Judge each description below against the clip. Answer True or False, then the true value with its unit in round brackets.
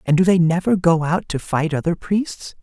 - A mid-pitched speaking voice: True (170 Hz)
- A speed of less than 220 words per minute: False (230 wpm)